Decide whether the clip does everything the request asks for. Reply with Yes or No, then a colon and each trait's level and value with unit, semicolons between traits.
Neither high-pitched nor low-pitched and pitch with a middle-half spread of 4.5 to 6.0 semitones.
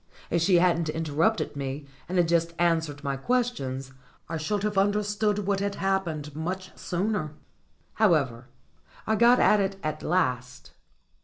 Yes: medium, 170 Hz; average, 5.0 semitones